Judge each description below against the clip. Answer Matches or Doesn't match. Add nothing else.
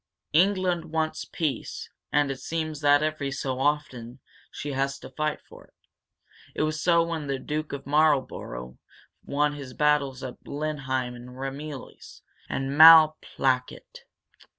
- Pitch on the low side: Doesn't match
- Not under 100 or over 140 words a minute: Matches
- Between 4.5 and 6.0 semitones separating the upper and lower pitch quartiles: Doesn't match